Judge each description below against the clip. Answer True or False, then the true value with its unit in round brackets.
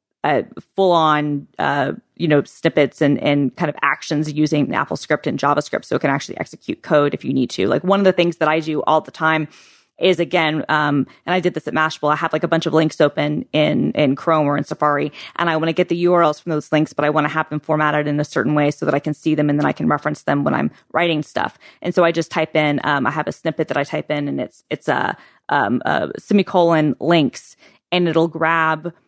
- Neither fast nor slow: False (255 wpm)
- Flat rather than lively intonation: True (1.9 semitones)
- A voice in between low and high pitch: True (155 Hz)